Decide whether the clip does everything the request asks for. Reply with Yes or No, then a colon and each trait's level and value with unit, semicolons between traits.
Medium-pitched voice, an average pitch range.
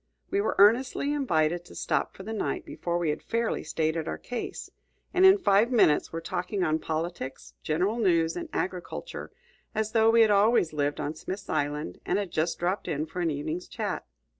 No: medium, 180 Hz; wide, 5.9 semitones